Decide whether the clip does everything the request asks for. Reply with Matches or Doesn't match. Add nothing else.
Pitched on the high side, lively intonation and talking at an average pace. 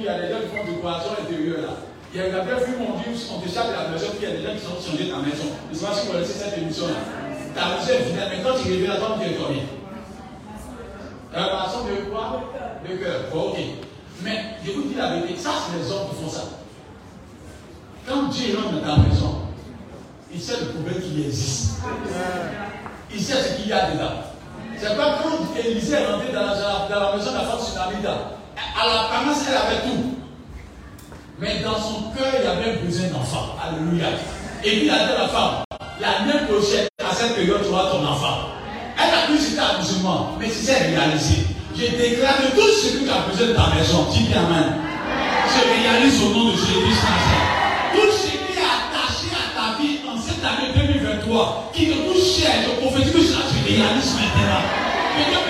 Doesn't match